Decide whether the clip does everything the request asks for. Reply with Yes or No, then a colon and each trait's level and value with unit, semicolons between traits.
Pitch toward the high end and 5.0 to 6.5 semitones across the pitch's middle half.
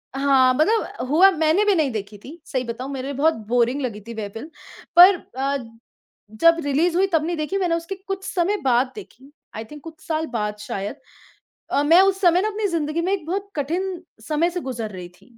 Yes: very high, 305 Hz; wide, 5.6 semitones